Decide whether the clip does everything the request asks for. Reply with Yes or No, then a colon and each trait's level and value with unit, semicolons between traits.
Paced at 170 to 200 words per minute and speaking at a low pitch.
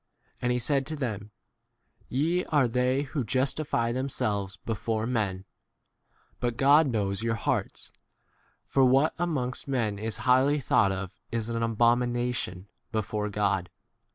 No: slow, 135 wpm; low, 120 Hz